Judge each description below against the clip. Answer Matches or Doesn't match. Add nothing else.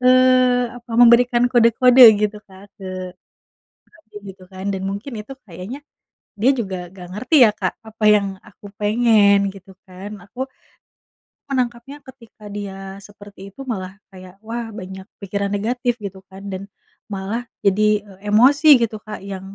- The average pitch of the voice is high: Matches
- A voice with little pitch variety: Doesn't match